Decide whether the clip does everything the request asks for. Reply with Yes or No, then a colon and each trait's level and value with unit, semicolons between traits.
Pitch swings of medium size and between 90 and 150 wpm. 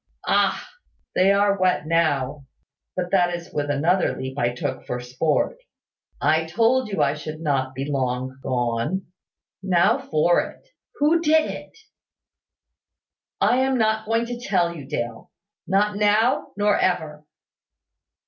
No: wide, 6.7 semitones; average, 140 wpm